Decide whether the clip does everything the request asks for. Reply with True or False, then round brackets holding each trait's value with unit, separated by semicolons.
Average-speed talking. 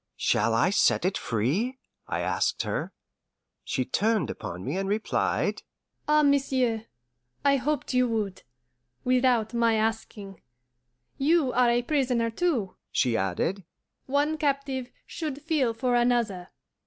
False (130 wpm)